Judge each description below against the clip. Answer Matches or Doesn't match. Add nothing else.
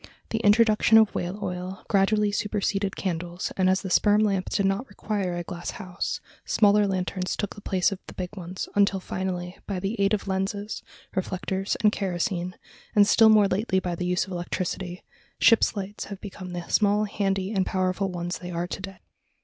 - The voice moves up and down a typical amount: Doesn't match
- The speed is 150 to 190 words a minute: Matches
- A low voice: Doesn't match